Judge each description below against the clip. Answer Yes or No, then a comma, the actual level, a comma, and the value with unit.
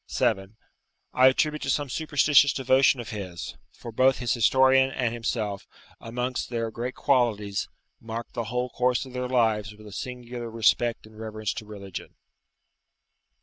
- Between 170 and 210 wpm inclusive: No, average, 150 wpm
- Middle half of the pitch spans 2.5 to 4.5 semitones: Yes, average, 2.9 semitones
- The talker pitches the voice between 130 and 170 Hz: No, low, 120 Hz